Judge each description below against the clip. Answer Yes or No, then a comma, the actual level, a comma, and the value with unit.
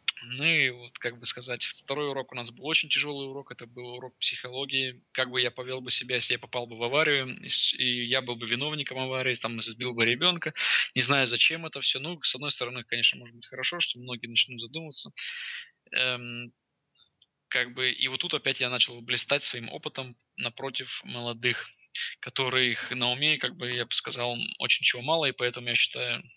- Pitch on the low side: Yes, low, 125 Hz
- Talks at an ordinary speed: No, fast, 195 wpm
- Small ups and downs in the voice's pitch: Yes, narrow, 2.0 semitones